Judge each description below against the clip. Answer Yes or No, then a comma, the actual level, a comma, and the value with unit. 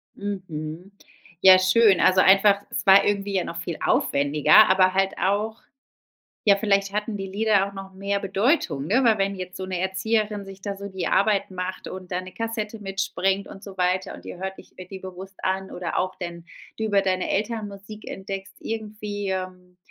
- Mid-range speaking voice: No, high, 195 Hz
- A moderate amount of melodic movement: No, narrow, 1.6 semitones